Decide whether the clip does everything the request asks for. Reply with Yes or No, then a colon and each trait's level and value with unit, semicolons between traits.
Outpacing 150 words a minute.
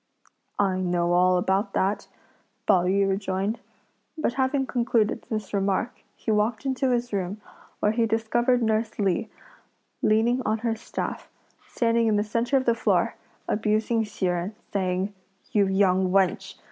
No: average, 145 wpm